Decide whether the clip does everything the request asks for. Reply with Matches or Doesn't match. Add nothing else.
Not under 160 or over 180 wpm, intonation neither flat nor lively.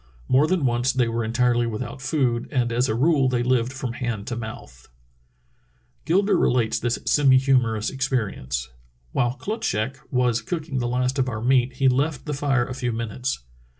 Doesn't match